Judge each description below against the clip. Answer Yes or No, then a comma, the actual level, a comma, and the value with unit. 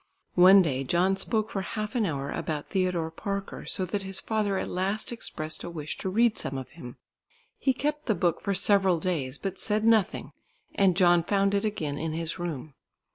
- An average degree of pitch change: Yes, average, 4.0 semitones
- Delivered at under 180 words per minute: No, average, 195 wpm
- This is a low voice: No, high, 190 Hz